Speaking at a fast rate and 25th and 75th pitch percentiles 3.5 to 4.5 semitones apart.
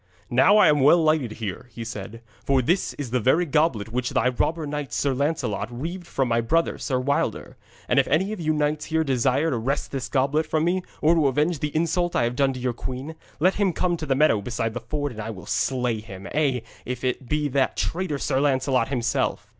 Yes: fast, 225 wpm; average, 4.2 semitones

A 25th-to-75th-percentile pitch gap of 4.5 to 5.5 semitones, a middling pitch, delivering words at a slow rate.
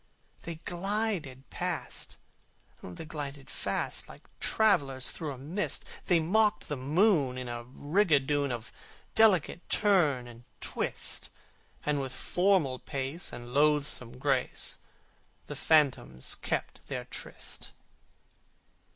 Yes: average, 5.1 semitones; medium, 145 Hz; slow, 110 wpm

